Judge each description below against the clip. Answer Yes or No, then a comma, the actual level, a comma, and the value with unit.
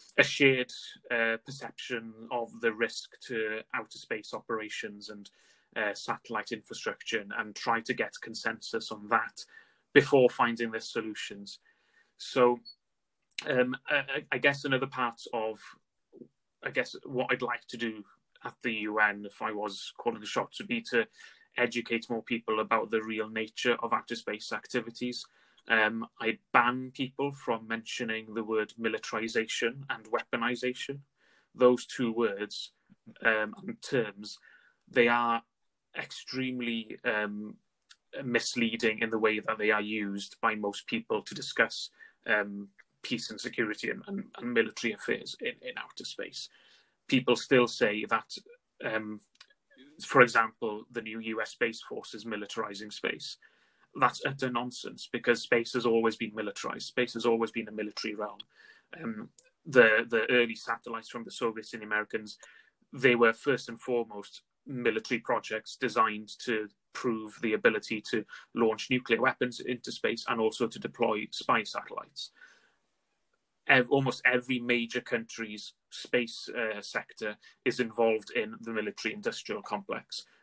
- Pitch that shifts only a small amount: Yes, narrow, 2.1 semitones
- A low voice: Yes, low, 115 Hz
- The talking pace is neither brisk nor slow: Yes, average, 145 wpm